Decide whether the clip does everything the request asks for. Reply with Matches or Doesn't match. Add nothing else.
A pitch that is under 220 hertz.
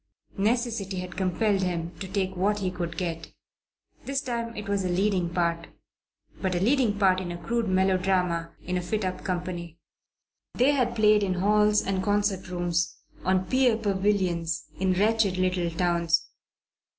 Matches